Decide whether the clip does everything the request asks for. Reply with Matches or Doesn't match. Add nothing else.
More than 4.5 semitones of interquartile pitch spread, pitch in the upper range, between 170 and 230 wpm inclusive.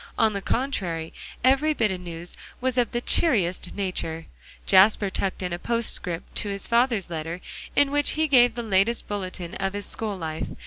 Matches